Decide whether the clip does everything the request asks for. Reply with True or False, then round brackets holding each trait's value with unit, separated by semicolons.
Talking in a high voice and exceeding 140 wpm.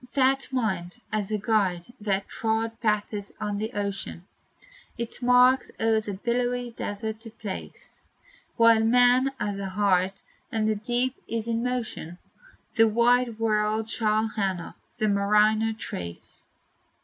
False (220 Hz; 135 wpm)